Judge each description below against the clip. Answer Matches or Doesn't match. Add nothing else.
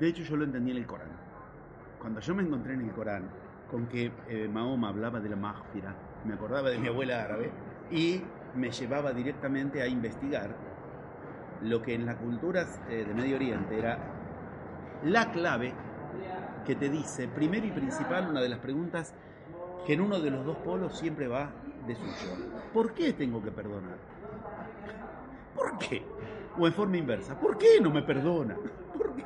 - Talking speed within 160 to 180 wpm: Matches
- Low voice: Matches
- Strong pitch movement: Matches